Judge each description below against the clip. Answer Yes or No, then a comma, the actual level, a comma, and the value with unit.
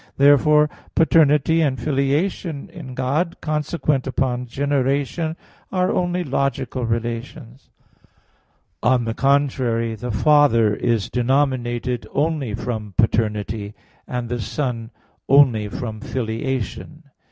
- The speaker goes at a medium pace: No, slow, 100 wpm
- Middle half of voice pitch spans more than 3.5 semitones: Yes, average, 4.0 semitones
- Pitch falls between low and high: No, low, 130 Hz